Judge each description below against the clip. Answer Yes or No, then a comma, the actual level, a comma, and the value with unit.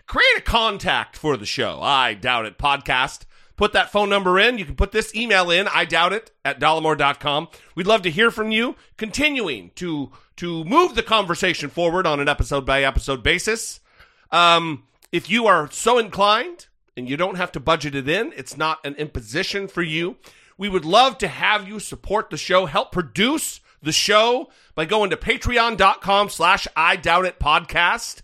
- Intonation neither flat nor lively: No, wide, 5.7 semitones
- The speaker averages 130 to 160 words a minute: No, average, 185 wpm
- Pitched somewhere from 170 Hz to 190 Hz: Yes, medium, 185 Hz